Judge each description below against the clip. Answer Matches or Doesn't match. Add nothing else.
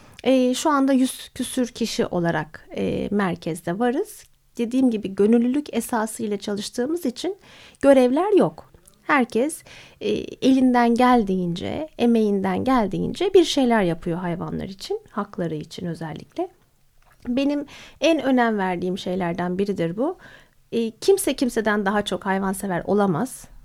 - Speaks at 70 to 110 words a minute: Matches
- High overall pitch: Matches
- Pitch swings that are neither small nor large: Doesn't match